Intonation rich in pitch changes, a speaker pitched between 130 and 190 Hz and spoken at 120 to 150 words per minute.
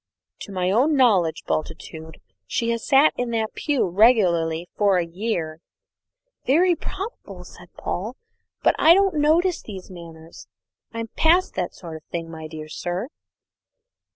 No: wide, 8.0 semitones; high, 200 Hz; average, 145 wpm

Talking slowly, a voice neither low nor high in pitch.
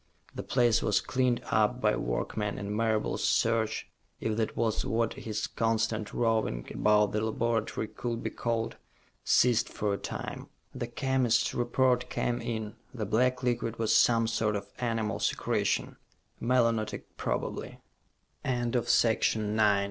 No: slow, 130 wpm; low, 115 Hz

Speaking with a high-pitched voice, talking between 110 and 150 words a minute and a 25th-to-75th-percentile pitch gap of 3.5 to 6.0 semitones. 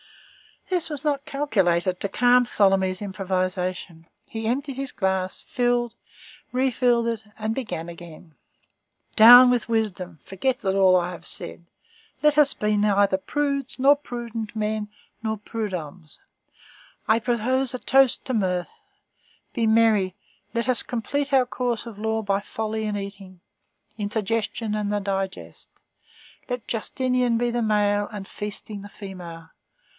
Yes: high, 220 Hz; average, 140 wpm; average, 4.2 semitones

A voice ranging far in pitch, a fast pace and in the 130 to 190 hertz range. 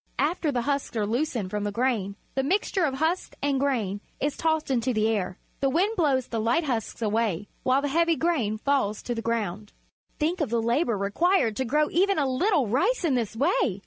No: wide, 5.7 semitones; fast, 210 wpm; very high, 260 Hz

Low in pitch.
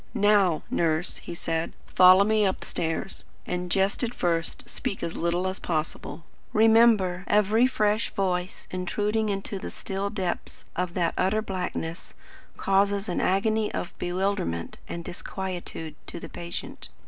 No: high, 190 Hz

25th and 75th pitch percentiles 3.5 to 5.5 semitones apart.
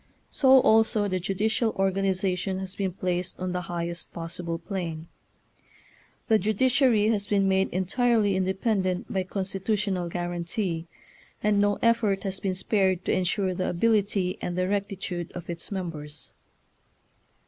No: narrow, 2.4 semitones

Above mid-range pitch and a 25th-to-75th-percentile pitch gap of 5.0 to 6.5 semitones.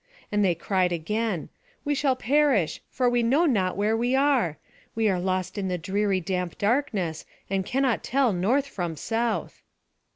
Yes: high, 210 Hz; wide, 5.5 semitones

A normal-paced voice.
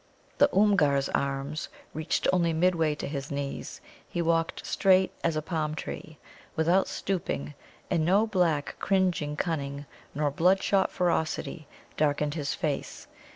No: slow, 130 wpm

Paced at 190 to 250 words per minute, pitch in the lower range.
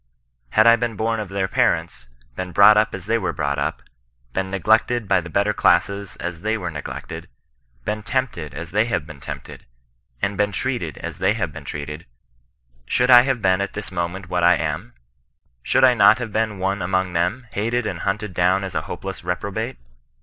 Yes: average, 200 wpm; low, 100 Hz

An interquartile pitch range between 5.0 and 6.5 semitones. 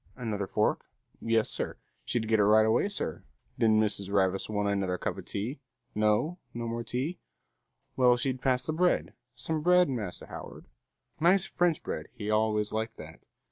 No: average, 4.2 semitones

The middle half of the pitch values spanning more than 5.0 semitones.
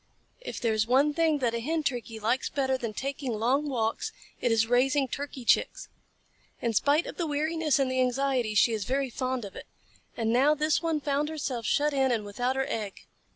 No: average, 3.7 semitones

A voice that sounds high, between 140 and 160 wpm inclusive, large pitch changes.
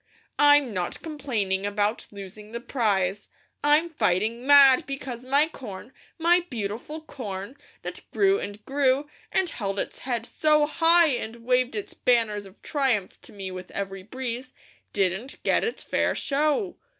Yes: high, 245 Hz; average, 150 wpm; wide, 6.0 semitones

